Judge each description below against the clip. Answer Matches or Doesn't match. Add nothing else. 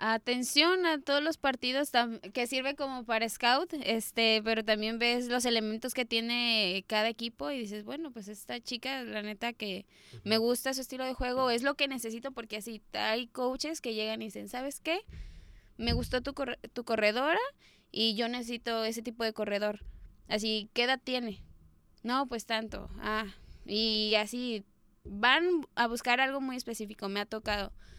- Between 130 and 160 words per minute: Doesn't match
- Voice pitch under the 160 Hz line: Doesn't match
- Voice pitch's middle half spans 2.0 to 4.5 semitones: Matches